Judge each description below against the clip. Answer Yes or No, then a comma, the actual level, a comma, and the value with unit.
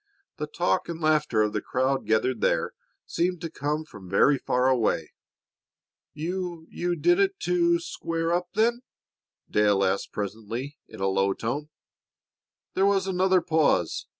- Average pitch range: No, wide, 8.2 semitones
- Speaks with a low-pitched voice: No, medium, 150 Hz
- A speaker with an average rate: Yes, average, 150 wpm